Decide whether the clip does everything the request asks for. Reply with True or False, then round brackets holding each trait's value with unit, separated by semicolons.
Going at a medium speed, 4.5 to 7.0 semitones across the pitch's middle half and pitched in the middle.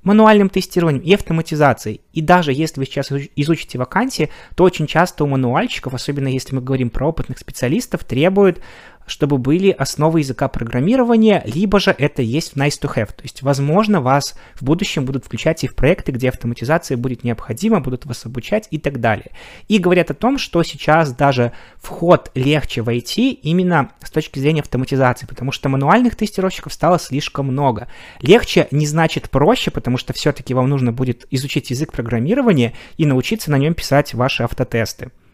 False (170 wpm; 4.8 semitones; 145 Hz)